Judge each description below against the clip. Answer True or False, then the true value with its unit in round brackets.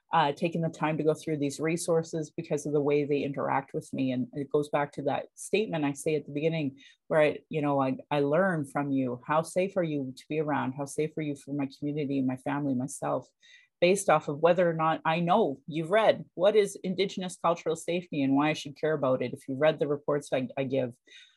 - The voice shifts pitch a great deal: False (2.8 semitones)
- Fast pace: True (240 wpm)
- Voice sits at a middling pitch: True (150 Hz)